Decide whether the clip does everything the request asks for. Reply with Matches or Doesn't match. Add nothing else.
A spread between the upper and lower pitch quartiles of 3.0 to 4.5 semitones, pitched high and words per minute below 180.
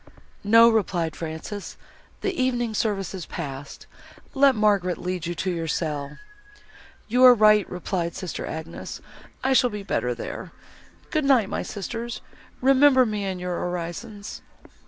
Doesn't match